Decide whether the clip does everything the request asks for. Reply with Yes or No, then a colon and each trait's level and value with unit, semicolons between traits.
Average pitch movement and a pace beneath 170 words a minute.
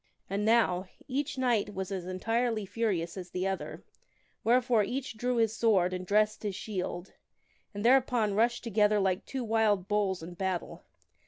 Yes: average, 3.6 semitones; average, 160 wpm